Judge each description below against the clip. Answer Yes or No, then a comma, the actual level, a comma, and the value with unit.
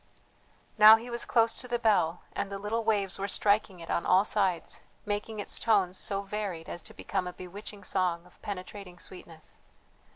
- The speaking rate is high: No, average, 185 wpm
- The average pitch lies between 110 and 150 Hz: No, high, 200 Hz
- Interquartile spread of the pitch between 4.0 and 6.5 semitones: No, average, 2.9 semitones